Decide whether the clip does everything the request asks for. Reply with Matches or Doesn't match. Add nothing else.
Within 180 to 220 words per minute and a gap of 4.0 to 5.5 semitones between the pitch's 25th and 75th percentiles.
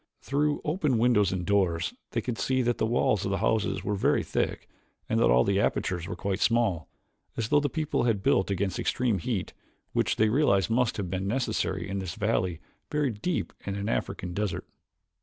Matches